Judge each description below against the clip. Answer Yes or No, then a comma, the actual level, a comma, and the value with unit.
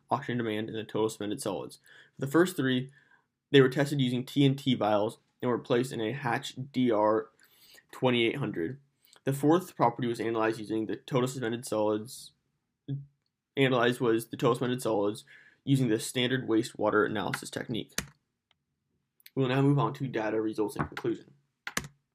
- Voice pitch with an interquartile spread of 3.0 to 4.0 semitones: Yes, average, 3.7 semitones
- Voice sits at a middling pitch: No, low, 125 Hz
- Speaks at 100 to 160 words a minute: Yes, average, 150 wpm